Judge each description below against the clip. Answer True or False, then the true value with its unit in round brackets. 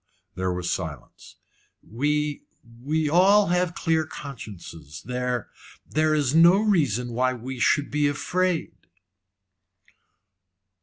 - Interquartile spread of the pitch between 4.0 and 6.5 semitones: True (5.3 semitones)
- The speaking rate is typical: False (105 wpm)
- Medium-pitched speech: True (145 Hz)